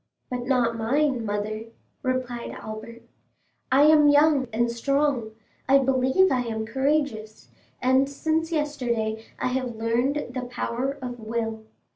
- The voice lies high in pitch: Yes, very high, 250 Hz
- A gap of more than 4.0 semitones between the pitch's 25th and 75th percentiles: No, average, 3.4 semitones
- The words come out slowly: Yes, slow, 130 wpm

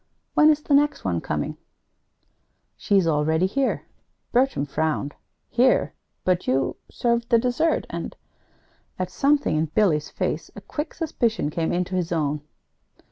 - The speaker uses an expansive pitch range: Yes, wide, 8.7 semitones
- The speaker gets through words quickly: No, average, 140 wpm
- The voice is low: No, medium, 185 Hz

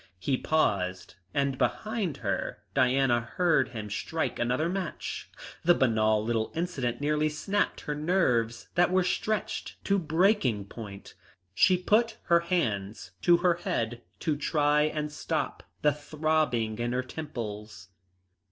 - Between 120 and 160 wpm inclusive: Yes, slow, 135 wpm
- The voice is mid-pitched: Yes, medium, 145 Hz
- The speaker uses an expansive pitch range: Yes, wide, 6.8 semitones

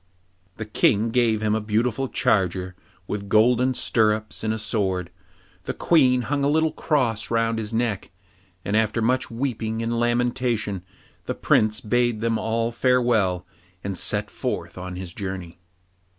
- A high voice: No, low, 110 Hz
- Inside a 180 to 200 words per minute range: No, average, 150 wpm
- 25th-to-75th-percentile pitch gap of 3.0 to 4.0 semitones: No, narrow, 2.6 semitones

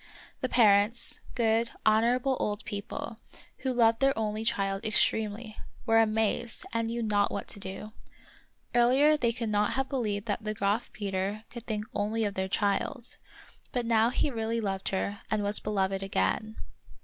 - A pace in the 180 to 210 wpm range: No, average, 160 wpm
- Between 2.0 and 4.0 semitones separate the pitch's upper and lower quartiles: Yes, narrow, 2.4 semitones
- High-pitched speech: Yes, high, 220 Hz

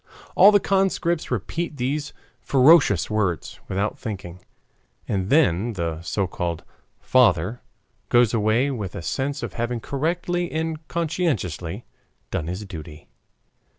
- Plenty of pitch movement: Yes, wide, 8.9 semitones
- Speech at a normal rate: No, slow, 120 wpm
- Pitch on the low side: Yes, low, 120 Hz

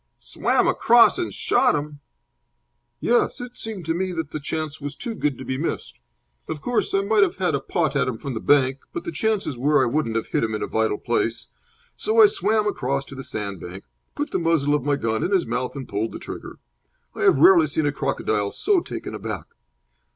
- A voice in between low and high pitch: Yes, medium, 145 Hz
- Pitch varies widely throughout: Yes, wide, 9.0 semitones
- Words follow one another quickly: Yes, fast, 220 wpm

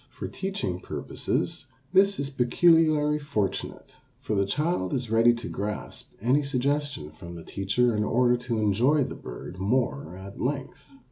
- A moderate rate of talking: Yes, average, 150 wpm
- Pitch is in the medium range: No, low, 125 Hz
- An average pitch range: No, wide, 6.5 semitones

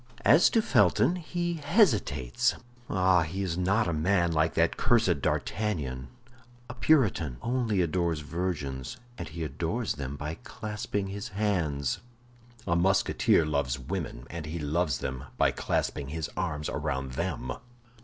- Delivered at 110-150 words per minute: Yes, average, 140 wpm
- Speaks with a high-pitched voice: No, very low, 85 Hz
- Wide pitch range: Yes, wide, 5.9 semitones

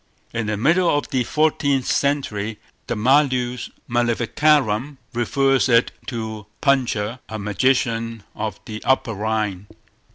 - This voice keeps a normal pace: No, slow, 120 wpm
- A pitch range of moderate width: Yes, average, 3.8 semitones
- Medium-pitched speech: No, low, 120 Hz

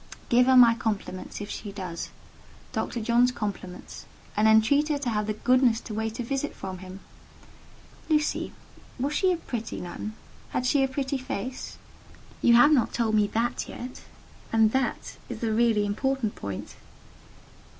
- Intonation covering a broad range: No, average, 3.6 semitones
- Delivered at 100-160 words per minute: Yes, average, 155 wpm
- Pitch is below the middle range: No, high, 230 Hz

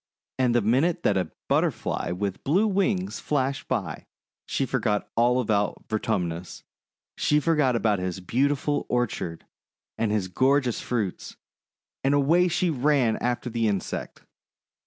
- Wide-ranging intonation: Yes, wide, 5.7 semitones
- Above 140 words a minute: No, slow, 135 wpm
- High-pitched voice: No, low, 120 Hz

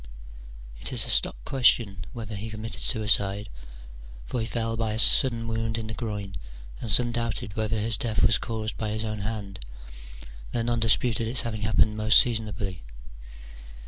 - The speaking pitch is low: Yes, low, 110 Hz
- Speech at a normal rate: Yes, average, 170 wpm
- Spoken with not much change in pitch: Yes, narrow, 1.5 semitones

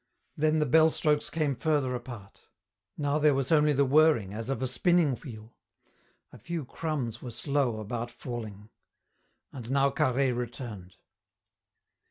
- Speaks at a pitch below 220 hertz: Yes, low, 135 Hz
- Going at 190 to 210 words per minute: No, average, 145 wpm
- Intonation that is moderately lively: Yes, average, 4.2 semitones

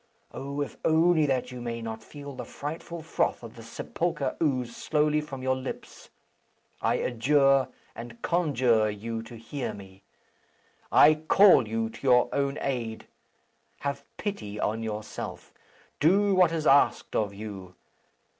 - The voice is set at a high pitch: No, low, 130 Hz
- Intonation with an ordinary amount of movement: Yes, average, 4.9 semitones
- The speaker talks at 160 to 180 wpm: No, average, 145 wpm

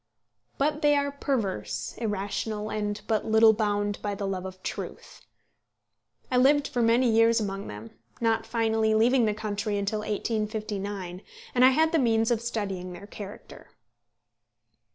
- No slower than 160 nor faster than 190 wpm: No, average, 150 wpm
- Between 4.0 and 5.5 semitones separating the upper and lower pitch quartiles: No, narrow, 2.4 semitones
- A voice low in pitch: No, high, 220 Hz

